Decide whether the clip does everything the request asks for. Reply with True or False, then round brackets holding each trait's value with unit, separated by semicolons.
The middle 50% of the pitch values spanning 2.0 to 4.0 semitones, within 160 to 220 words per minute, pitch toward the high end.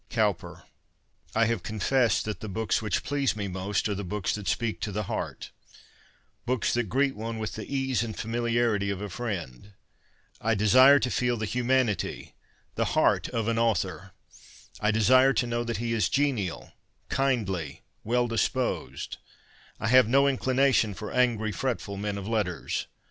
False (3.3 semitones; 165 wpm; 115 Hz)